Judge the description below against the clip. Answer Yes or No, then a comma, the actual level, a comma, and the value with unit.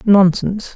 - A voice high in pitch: Yes, high, 195 Hz